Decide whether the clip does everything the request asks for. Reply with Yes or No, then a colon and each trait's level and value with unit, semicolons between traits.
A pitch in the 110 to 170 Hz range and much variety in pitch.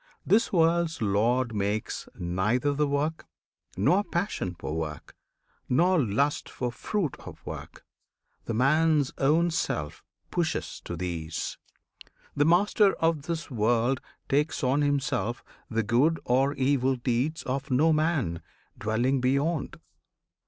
Yes: low, 135 Hz; wide, 5.9 semitones